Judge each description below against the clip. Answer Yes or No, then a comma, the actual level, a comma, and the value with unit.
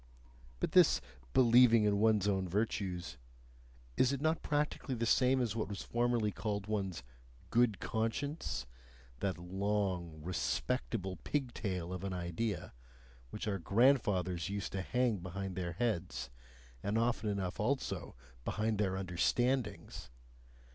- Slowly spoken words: Yes, slow, 125 wpm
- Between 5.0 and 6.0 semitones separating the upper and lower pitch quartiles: No, average, 4.2 semitones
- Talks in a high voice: No, low, 100 Hz